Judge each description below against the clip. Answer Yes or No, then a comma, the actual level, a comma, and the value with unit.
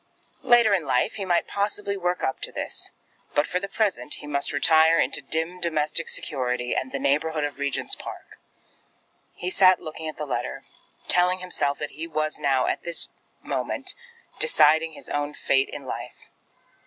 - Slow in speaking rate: No, average, 170 wpm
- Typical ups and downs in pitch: Yes, average, 4.0 semitones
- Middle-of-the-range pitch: Yes, medium, 160 Hz